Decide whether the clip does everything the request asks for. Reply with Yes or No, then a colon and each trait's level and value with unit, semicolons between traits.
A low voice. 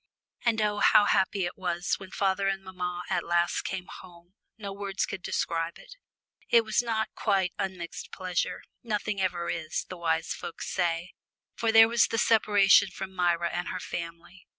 No: medium, 185 Hz